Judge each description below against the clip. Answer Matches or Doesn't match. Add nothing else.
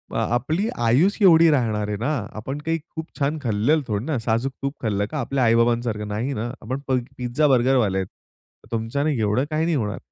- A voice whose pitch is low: Matches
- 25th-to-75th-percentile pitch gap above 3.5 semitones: Matches